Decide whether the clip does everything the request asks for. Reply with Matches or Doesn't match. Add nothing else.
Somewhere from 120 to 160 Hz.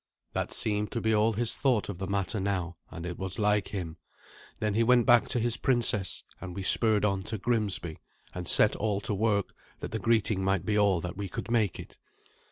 Doesn't match